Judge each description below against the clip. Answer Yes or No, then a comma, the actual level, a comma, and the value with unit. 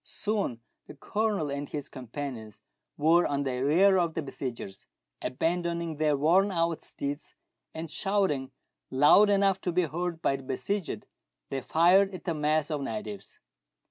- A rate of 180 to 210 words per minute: No, average, 150 wpm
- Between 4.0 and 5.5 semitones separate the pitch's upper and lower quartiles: Yes, average, 4.5 semitones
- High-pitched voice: No, medium, 155 Hz